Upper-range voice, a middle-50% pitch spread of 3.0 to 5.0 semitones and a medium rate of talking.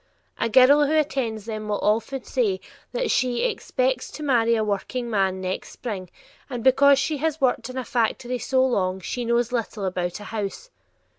Yes: high, 240 Hz; average, 4.1 semitones; average, 175 wpm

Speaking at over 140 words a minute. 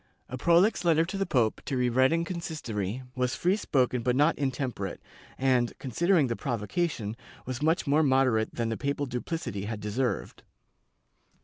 Yes: average, 170 wpm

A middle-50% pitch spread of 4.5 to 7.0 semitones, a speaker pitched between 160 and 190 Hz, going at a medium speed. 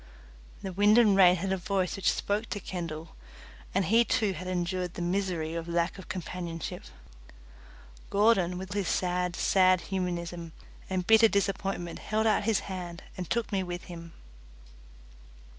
No: narrow, 2.4 semitones; medium, 185 Hz; average, 155 wpm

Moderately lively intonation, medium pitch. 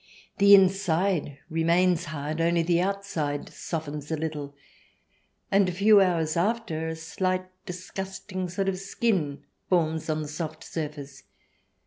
Yes: average, 3.4 semitones; medium, 170 Hz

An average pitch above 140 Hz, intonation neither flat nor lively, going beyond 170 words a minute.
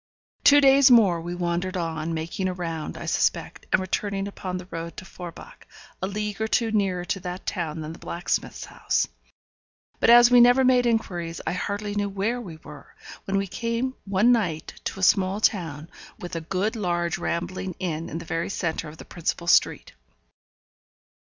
Yes: medium, 185 Hz; average, 3.9 semitones; average, 185 wpm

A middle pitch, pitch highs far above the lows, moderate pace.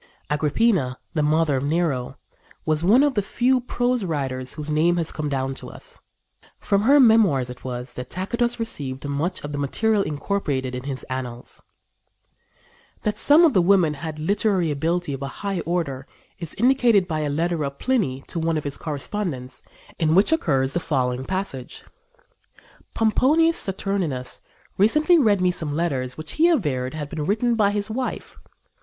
Yes: medium, 165 Hz; wide, 7.0 semitones; average, 170 wpm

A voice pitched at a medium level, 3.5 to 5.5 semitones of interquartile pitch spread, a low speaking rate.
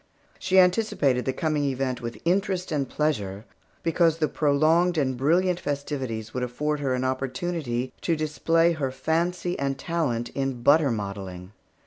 No: medium, 145 Hz; average, 4.6 semitones; average, 145 wpm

